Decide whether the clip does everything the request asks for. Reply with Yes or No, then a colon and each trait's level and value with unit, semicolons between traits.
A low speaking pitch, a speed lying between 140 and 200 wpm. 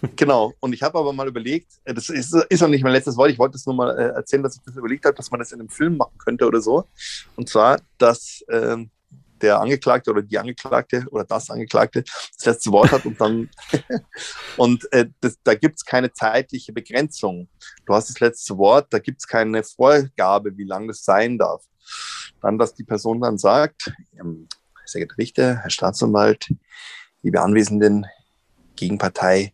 Yes: low, 120 Hz; fast, 190 wpm